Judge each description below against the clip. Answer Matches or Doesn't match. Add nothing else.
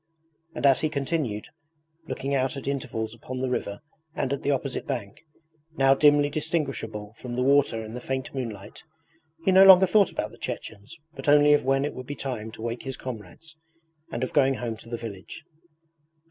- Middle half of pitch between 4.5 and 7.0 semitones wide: Doesn't match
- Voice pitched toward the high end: Doesn't match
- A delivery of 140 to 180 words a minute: Doesn't match